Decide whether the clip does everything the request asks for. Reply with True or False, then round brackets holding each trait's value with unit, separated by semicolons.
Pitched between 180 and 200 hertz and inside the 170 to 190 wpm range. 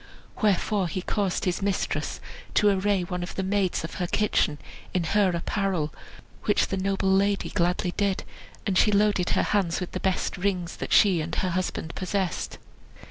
True (190 Hz; 175 wpm)